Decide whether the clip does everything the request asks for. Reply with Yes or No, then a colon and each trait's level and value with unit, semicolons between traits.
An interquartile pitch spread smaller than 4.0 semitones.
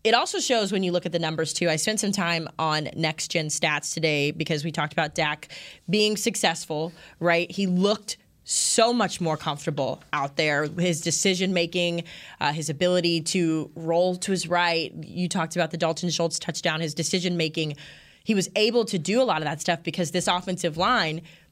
Yes: narrow, 2.6 semitones